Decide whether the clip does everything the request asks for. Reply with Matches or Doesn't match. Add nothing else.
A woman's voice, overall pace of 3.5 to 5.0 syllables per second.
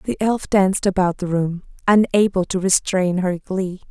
Matches